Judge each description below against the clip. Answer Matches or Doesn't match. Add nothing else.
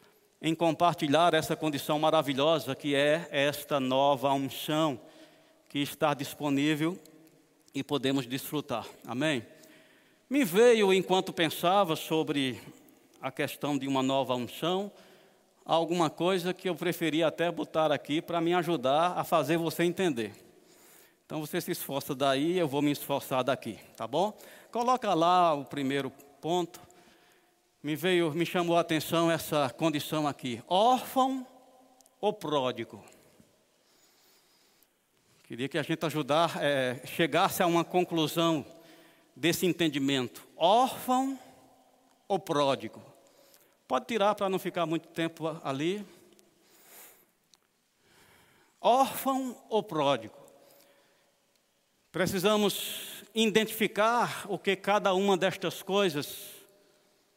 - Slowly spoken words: Matches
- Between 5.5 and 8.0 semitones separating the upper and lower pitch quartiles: Doesn't match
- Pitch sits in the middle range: Matches